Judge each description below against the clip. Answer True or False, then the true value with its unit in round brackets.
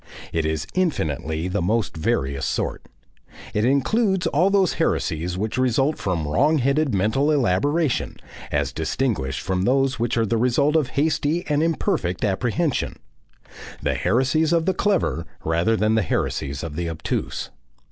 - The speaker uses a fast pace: False (145 wpm)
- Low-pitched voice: True (115 Hz)